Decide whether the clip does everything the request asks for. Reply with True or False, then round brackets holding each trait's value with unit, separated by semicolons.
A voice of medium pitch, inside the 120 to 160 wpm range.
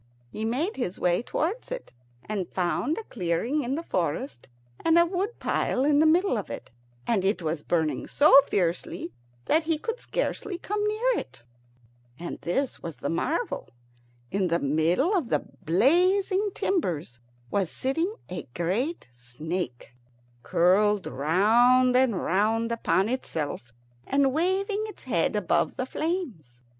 False (230 Hz; 150 wpm)